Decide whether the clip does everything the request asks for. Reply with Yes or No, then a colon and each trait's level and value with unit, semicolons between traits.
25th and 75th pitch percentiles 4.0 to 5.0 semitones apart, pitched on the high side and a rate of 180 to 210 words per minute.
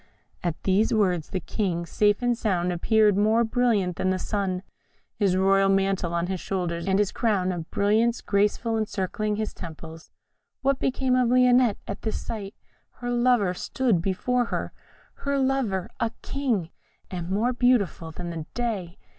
No: average, 4.5 semitones; high, 200 Hz; average, 160 wpm